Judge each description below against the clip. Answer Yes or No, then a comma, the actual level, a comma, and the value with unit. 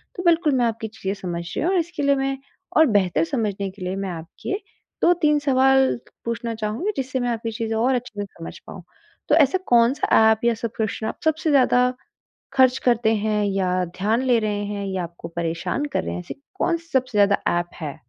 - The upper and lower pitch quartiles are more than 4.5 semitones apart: Yes, average, 5.1 semitones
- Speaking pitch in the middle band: No, high, 230 Hz